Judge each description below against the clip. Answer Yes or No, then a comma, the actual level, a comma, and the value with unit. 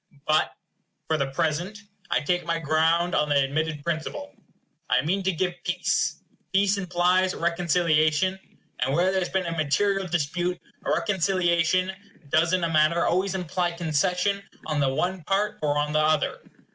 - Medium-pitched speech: Yes, medium, 170 Hz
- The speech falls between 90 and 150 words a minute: No, average, 160 wpm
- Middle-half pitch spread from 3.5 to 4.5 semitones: No, average, 3.0 semitones